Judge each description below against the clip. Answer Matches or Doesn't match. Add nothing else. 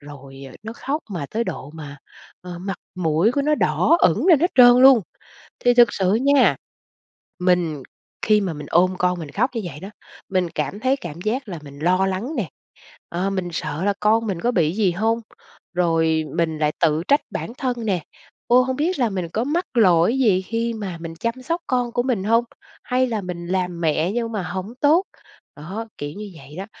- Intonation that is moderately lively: Doesn't match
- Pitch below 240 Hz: Matches